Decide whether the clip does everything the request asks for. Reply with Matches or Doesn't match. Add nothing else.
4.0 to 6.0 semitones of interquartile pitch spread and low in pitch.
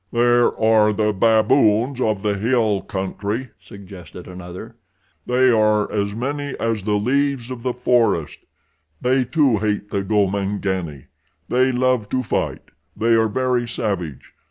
Doesn't match